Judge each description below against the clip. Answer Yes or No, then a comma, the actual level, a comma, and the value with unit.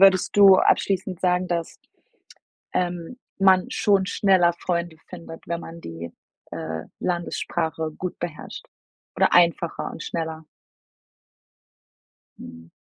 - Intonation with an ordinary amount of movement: No, narrow, 2.3 semitones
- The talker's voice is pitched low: No, medium, 175 Hz